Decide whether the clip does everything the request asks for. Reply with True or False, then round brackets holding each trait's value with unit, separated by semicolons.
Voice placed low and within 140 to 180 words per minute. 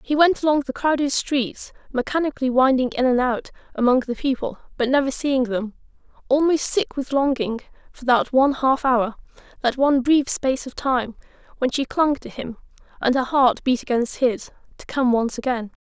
False (265 Hz; 170 wpm)